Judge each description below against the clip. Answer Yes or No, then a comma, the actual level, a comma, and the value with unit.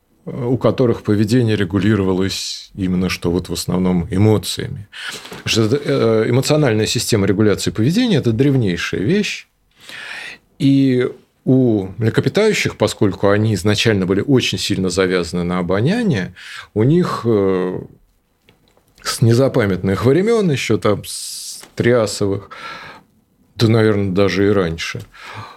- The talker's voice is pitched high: No, low, 110 Hz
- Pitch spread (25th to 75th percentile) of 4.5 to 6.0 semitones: Yes, average, 5.2 semitones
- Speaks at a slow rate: Yes, slow, 100 wpm